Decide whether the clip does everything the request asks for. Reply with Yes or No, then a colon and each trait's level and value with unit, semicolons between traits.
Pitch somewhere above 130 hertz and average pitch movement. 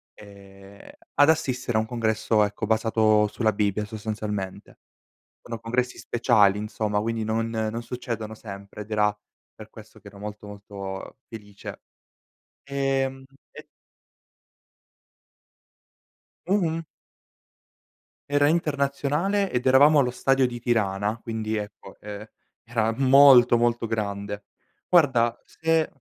No: low, 110 Hz; average, 3.9 semitones